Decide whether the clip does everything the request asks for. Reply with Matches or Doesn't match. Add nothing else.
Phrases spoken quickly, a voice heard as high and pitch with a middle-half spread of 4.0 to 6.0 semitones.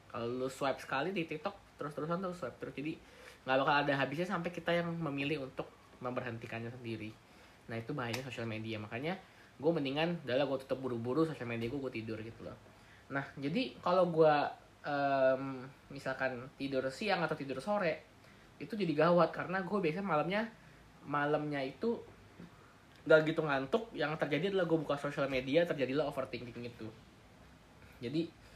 Doesn't match